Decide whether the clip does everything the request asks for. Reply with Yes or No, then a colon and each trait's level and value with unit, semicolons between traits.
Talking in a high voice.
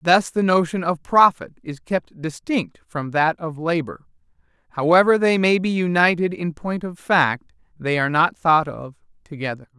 No: medium, 170 Hz